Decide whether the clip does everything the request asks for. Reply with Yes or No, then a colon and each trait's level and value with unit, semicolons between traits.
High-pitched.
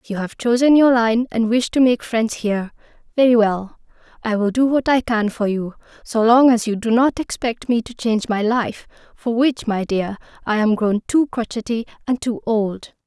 Yes: high, 230 Hz